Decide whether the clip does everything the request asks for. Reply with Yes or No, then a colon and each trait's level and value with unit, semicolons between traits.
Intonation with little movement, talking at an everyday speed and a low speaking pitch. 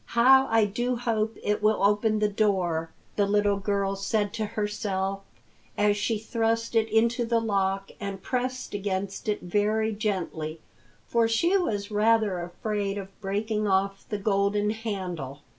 No: narrow, 2.2 semitones; average, 150 wpm; high, 210 Hz